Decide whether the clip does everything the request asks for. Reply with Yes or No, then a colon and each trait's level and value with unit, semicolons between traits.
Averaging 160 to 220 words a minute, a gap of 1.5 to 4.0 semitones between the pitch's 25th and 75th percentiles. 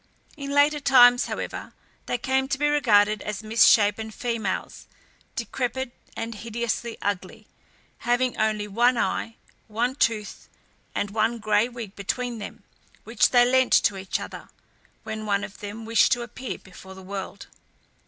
No: average, 145 wpm; average, 2.9 semitones